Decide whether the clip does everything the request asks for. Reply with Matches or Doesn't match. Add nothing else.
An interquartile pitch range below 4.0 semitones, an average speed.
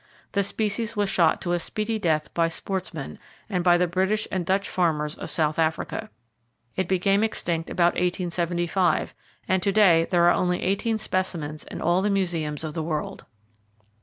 Matches